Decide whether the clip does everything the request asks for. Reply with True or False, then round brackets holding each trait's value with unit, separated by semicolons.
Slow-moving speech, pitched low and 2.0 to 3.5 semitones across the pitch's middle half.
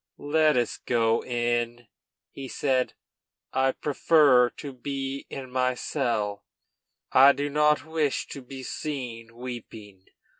True (120 wpm; 130 Hz; 2.9 semitones)